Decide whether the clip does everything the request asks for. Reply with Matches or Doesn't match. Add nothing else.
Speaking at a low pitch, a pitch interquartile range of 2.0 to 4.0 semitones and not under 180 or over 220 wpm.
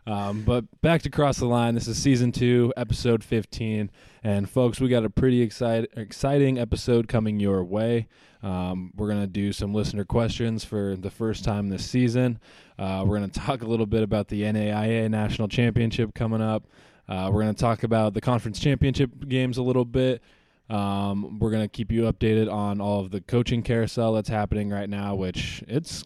Matches